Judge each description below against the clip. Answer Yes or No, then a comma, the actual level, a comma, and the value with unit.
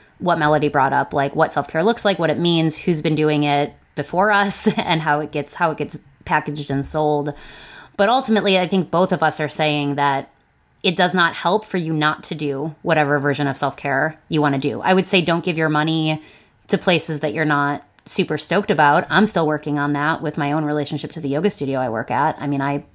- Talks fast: Yes, fast, 240 wpm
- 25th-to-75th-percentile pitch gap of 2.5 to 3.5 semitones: Yes, average, 3.2 semitones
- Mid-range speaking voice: Yes, medium, 155 Hz